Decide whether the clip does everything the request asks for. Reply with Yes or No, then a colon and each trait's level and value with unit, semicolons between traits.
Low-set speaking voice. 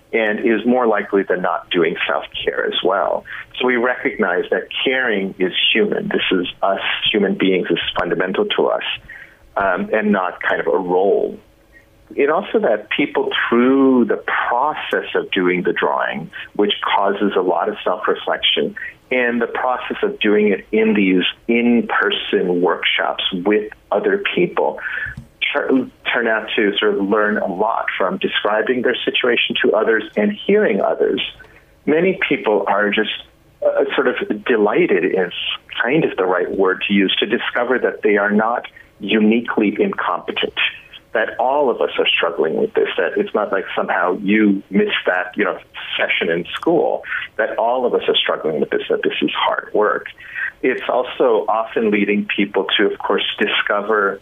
Yes: low, 125 Hz